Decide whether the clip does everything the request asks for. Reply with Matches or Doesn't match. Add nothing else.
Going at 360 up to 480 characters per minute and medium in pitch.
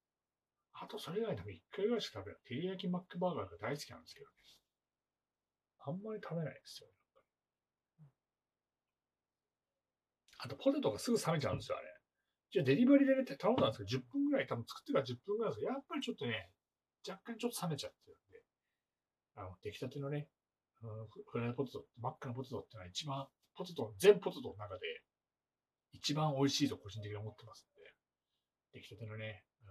Matches